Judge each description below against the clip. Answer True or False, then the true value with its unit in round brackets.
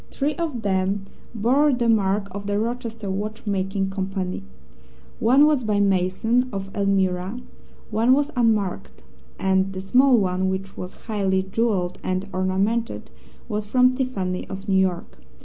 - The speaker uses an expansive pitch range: False (3.5 semitones)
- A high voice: True (200 Hz)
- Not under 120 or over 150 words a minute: True (140 wpm)